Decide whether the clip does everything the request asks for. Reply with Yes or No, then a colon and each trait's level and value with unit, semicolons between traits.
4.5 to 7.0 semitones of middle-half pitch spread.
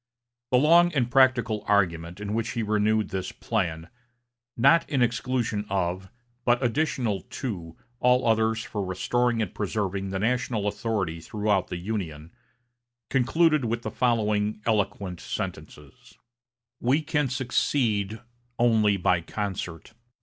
No: average, 4.1 semitones